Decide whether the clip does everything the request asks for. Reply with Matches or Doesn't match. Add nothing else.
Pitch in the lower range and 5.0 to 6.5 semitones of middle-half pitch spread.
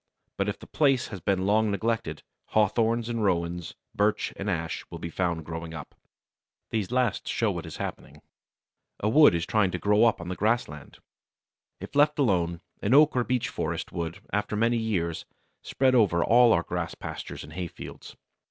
Matches